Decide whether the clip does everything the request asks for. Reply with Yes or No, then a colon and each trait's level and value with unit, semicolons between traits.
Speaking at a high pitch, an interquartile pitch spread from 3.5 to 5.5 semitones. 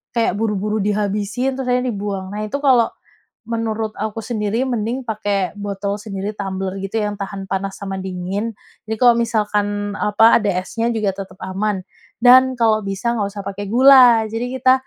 No: high, 210 Hz; average, 2.7 semitones